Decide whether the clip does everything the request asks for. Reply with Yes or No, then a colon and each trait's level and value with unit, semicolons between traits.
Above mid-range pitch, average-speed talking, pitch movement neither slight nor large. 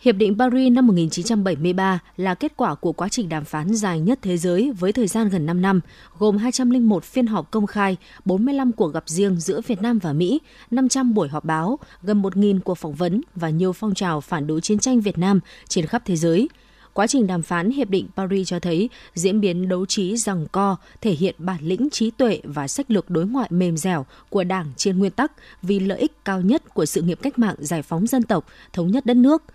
Yes: high, 195 Hz; average, 225 wpm; average, 4.9 semitones